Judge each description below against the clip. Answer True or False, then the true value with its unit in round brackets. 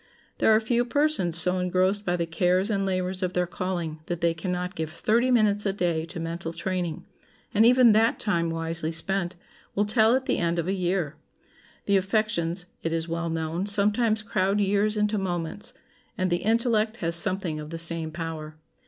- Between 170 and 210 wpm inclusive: True (190 wpm)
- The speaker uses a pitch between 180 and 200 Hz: True (185 Hz)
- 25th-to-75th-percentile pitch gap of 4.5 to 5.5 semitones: False (3.8 semitones)